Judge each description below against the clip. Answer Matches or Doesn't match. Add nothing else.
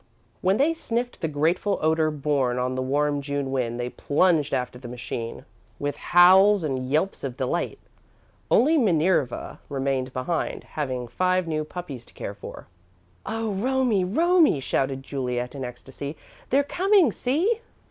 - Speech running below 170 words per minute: Matches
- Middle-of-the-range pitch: Matches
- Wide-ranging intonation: Matches